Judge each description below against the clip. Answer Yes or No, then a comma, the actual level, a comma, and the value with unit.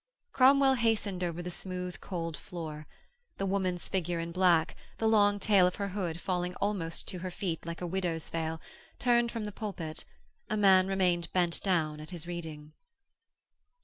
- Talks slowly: No, average, 170 wpm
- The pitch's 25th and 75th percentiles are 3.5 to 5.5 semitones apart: No, average, 3.1 semitones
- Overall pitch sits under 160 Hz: No, medium, 180 Hz